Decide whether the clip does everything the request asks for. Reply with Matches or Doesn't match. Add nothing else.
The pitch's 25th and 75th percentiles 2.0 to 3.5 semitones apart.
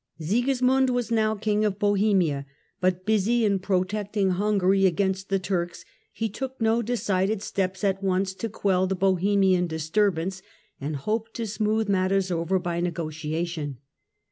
Matches